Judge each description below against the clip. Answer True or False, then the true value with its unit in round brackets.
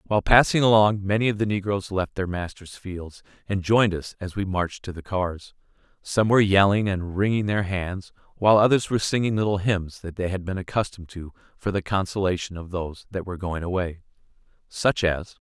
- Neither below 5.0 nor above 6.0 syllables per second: True (5.6 syllables/s)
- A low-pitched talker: True (95 Hz)